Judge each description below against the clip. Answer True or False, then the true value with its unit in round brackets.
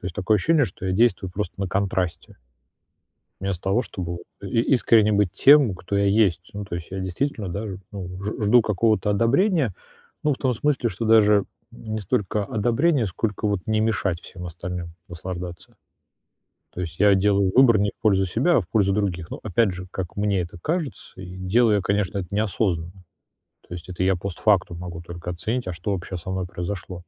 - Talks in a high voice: False (100 Hz)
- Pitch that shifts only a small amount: False (3.3 semitones)